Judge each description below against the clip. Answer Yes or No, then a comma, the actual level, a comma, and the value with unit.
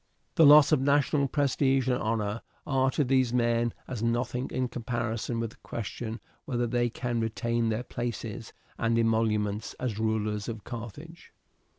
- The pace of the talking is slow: No, average, 155 wpm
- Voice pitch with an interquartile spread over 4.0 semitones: No, narrow, 2.4 semitones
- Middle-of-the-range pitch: No, low, 120 Hz